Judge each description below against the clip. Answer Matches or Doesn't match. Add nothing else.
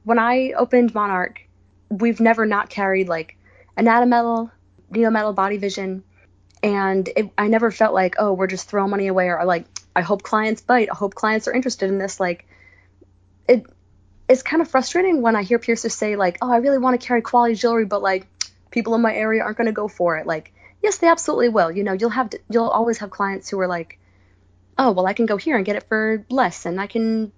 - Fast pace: Matches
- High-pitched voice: Matches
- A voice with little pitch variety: Doesn't match